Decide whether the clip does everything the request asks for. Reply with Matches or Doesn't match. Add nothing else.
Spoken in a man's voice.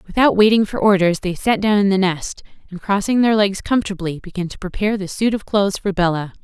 Doesn't match